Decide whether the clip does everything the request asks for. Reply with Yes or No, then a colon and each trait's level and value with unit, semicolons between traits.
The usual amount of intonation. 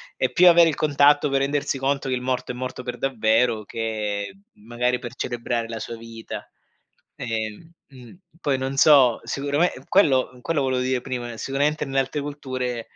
Yes: average, 3.0 semitones